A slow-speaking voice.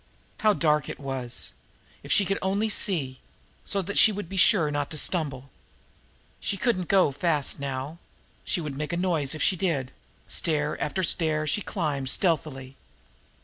No: average, 165 wpm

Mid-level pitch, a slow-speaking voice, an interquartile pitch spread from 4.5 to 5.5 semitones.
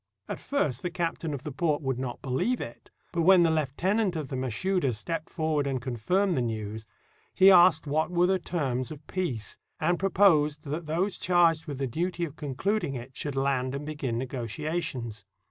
No: medium, 150 Hz; average, 185 wpm; average, 5.0 semitones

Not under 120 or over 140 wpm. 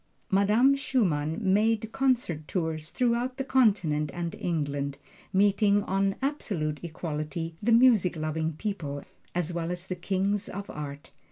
Yes: slow, 135 wpm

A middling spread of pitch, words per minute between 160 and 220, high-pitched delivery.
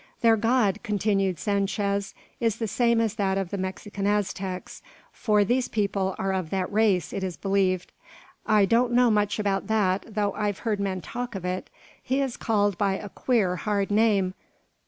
No: narrow, 2.3 semitones; average, 180 wpm; high, 205 Hz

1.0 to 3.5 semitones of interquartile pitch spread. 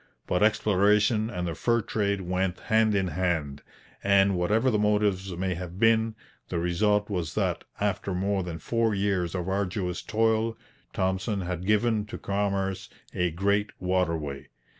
Yes: average, 2.8 semitones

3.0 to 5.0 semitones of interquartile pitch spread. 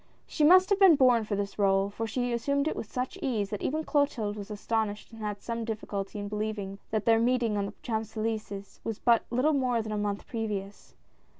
Yes: average, 3.3 semitones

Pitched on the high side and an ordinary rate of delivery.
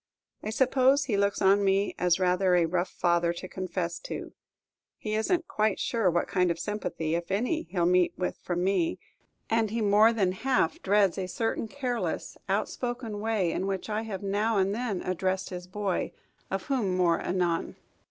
Yes: high, 195 Hz; average, 185 wpm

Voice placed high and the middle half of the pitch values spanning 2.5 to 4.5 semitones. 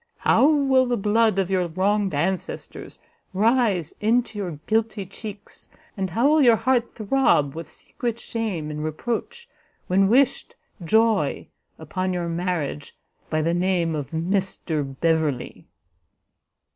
No: high, 195 Hz; wide, 5.5 semitones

